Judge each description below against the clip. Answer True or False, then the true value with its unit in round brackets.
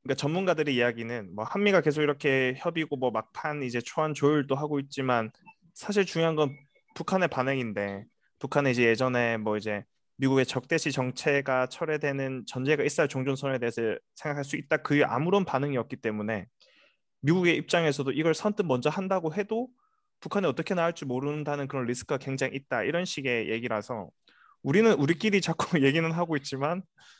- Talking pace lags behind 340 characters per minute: False (395 characters per minute)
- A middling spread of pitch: True (4.3 semitones)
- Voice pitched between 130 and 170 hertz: True (140 Hz)